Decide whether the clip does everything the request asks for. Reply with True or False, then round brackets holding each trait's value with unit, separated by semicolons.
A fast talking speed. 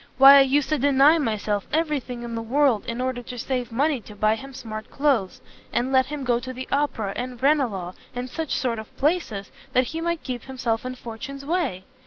True (215 wpm)